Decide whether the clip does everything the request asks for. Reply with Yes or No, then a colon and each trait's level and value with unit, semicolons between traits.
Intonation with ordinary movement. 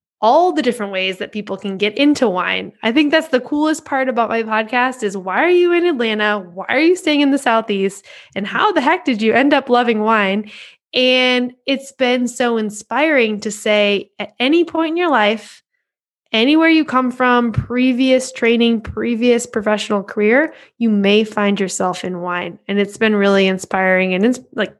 Yes: average, 4.2 semitones